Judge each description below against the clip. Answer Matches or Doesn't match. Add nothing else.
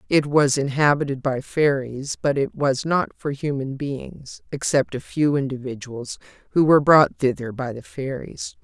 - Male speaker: Doesn't match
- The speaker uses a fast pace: Doesn't match